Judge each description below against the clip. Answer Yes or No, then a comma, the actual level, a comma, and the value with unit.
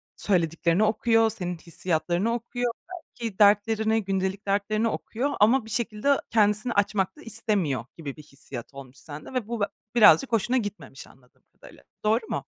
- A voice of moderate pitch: No, high, 210 Hz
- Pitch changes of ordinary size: Yes, average, 4.4 semitones